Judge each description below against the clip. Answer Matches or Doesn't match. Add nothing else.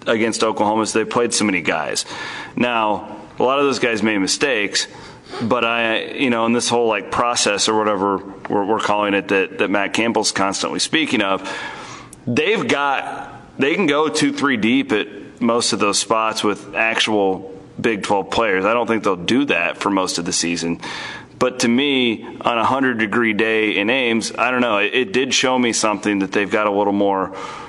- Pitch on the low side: Matches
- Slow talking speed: Doesn't match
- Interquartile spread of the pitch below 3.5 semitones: Matches